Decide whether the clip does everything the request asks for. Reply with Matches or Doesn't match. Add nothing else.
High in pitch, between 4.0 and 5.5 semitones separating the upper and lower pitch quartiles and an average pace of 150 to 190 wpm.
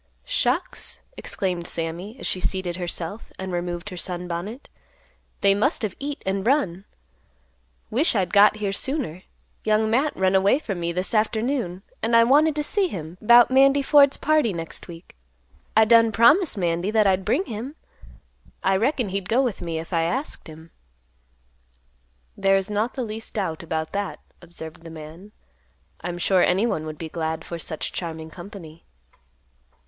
Matches